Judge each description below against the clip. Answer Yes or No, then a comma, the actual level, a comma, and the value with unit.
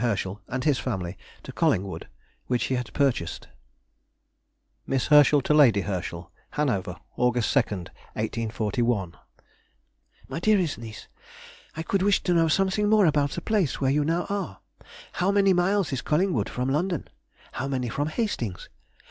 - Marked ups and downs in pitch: Yes, wide, 7.5 semitones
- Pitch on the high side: No, low, 135 Hz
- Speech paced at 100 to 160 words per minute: Yes, average, 150 wpm